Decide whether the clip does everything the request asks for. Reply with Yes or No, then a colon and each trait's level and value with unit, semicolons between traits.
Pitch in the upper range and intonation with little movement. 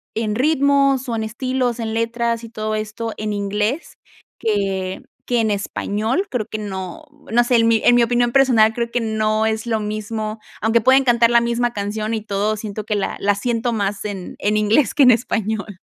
Yes: high, 220 Hz; narrow, 2.1 semitones